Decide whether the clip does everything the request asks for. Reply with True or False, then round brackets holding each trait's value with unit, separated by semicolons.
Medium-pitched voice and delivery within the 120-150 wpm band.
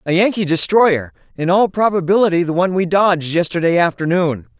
True (180 Hz; 145 wpm)